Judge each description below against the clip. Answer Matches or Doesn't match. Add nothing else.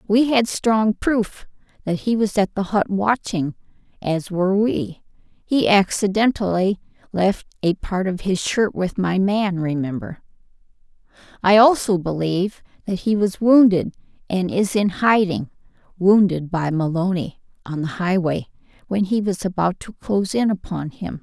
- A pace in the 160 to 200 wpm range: Doesn't match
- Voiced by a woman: Matches